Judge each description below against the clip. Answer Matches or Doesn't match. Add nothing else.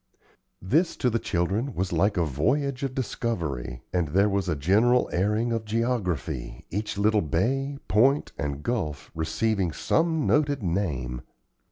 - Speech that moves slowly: Doesn't match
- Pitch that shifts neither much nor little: Doesn't match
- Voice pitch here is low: Matches